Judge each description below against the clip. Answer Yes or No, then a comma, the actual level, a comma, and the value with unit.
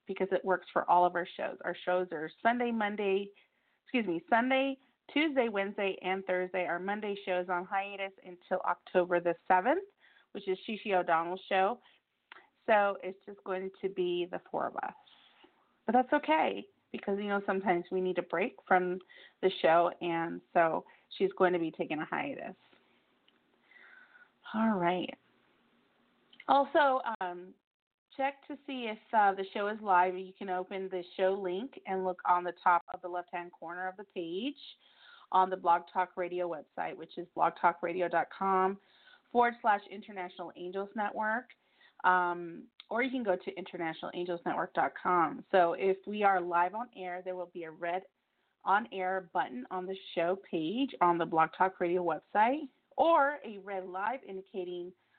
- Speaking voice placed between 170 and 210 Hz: Yes, medium, 185 Hz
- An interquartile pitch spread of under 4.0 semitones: Yes, average, 2.9 semitones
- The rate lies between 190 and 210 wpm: No, average, 165 wpm